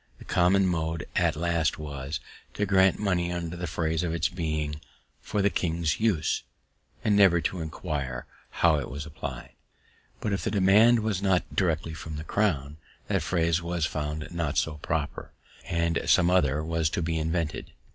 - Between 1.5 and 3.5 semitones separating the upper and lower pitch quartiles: Yes, average, 2.8 semitones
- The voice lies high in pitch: No, very low, 85 Hz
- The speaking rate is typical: Yes, average, 170 wpm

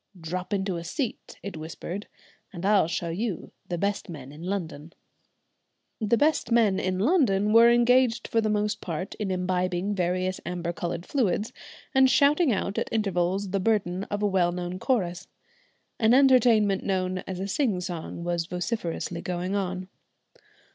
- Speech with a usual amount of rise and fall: Yes, average, 3.6 semitones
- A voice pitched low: No, high, 190 Hz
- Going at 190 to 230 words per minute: No, average, 160 wpm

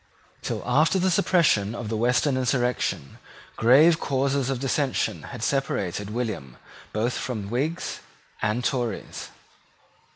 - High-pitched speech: No, low, 125 Hz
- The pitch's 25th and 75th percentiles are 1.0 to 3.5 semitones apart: No, average, 4.0 semitones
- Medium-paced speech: No, slow, 120 wpm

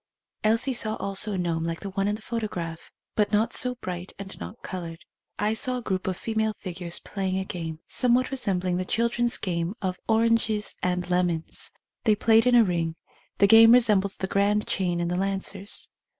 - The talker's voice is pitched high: Yes, high, 195 Hz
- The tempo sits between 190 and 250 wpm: Yes, average, 195 wpm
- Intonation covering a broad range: No, average, 3.8 semitones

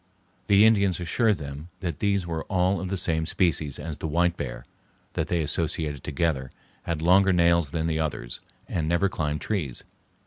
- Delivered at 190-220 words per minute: No, average, 175 wpm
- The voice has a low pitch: Yes, very low, 85 Hz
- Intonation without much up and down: No, average, 3.3 semitones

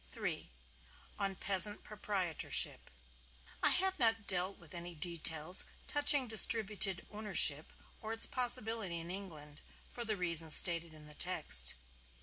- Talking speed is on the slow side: Yes, slow, 130 wpm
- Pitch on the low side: No, high, 190 Hz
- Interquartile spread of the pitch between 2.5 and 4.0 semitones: No, average, 4.7 semitones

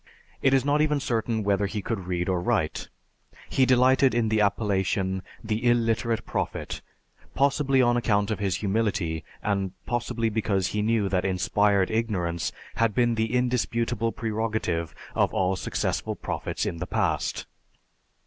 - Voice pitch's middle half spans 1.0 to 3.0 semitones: No, average, 3.7 semitones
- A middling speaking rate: Yes, average, 150 wpm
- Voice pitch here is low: Yes, low, 110 Hz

